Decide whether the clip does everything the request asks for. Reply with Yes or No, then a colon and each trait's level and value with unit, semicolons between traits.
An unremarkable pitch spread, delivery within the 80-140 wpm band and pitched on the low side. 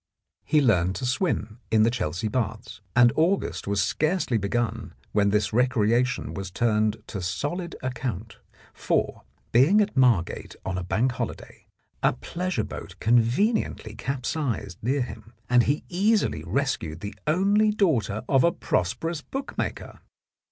No: wide, 6.4 semitones; slow, 135 wpm; low, 120 Hz